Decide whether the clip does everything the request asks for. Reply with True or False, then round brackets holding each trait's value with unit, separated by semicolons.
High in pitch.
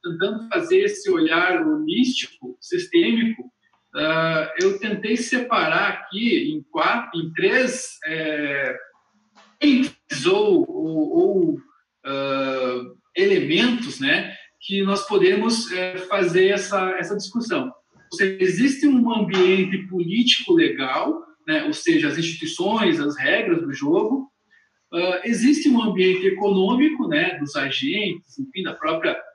True (230 Hz)